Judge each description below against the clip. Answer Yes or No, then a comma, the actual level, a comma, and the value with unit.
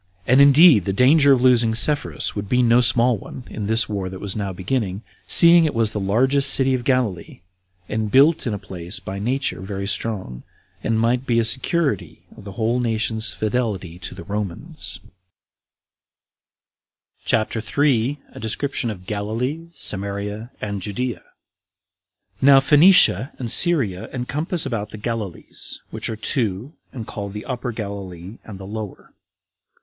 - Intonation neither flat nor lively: Yes, average, 4.3 semitones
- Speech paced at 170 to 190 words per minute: No, average, 155 wpm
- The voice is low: Yes, low, 110 Hz